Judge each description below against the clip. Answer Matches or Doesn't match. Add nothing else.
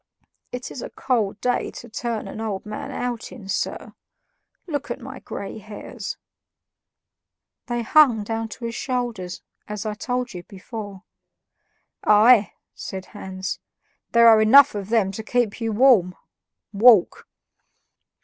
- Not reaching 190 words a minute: Matches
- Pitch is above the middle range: Matches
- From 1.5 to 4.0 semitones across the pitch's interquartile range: Matches